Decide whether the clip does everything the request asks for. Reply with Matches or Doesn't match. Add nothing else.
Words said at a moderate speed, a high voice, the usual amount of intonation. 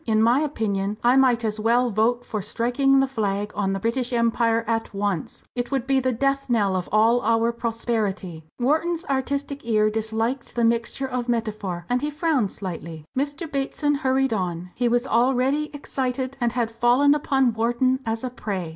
Matches